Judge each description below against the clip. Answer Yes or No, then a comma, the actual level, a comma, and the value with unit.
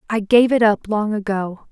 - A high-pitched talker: Yes, high, 210 Hz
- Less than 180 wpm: No, fast, 210 wpm